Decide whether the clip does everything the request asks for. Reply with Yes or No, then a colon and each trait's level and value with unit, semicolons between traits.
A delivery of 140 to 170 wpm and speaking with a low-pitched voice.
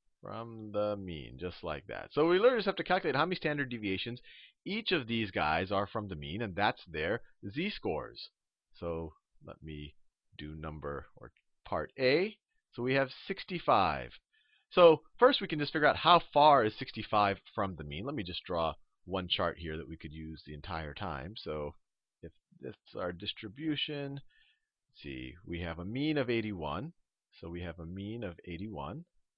No: average, 185 wpm; low, 105 Hz